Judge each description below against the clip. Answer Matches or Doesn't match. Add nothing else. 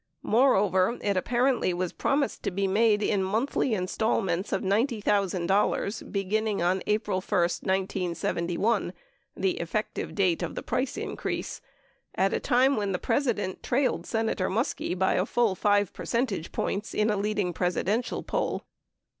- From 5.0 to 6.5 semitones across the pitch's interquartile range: Doesn't match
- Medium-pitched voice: Doesn't match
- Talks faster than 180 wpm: Doesn't match